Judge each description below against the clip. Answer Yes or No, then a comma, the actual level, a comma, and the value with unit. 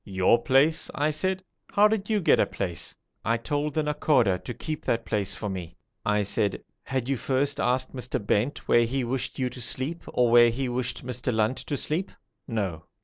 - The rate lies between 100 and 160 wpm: No, average, 200 wpm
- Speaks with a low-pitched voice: Yes, low, 125 Hz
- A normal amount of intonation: Yes, average, 4.7 semitones